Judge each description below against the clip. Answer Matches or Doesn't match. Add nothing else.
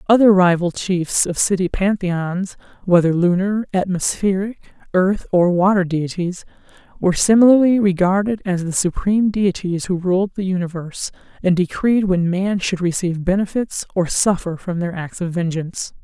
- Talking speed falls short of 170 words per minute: Matches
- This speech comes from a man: Doesn't match